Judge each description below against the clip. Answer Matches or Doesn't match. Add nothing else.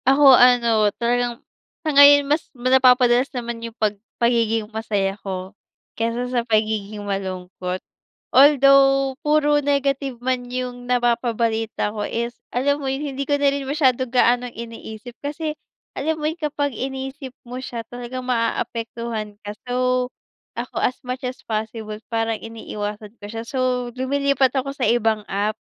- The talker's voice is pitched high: Matches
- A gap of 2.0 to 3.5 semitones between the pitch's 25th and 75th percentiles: Matches